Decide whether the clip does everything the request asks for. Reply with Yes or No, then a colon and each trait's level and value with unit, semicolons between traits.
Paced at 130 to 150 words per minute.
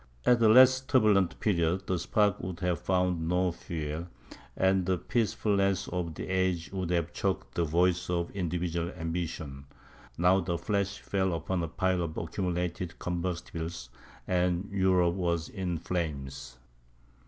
Yes: average, 145 wpm